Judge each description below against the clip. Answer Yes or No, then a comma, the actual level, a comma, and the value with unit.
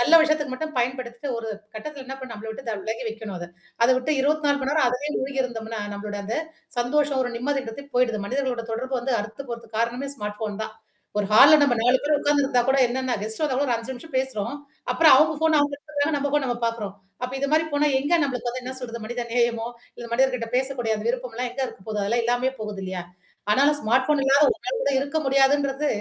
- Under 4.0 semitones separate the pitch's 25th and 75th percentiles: Yes, average, 3.5 semitones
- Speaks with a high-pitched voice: Yes, very high, 255 Hz